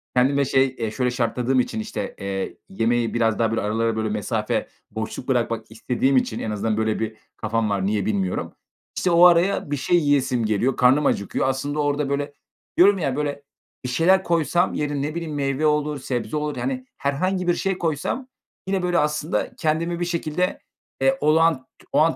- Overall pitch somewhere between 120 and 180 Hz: Yes, medium, 140 Hz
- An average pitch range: No, wide, 6.0 semitones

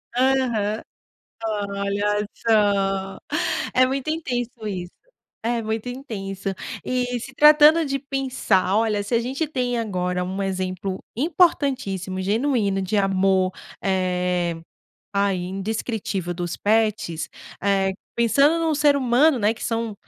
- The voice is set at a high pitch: Yes, high, 215 Hz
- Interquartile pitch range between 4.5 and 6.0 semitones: Yes, average, 4.8 semitones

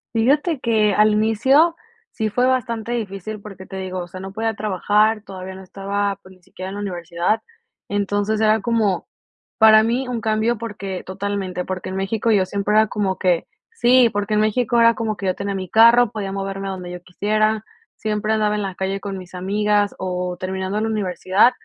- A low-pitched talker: No, high, 205 Hz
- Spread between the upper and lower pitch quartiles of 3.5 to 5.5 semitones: No, narrow, 2.5 semitones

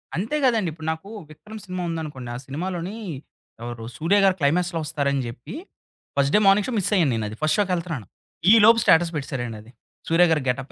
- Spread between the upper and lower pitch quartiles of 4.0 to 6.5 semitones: Yes, average, 5.2 semitones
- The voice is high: No, medium, 165 Hz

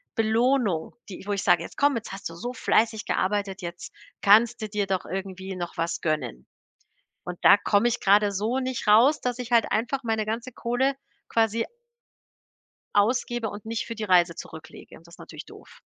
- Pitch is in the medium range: No, high, 210 Hz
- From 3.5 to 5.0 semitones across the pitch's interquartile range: Yes, average, 3.8 semitones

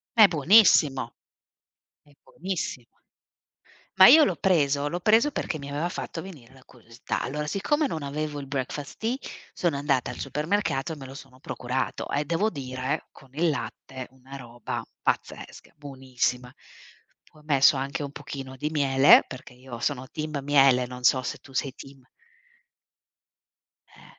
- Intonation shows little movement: No, average, 3.0 semitones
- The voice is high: No, medium, 140 Hz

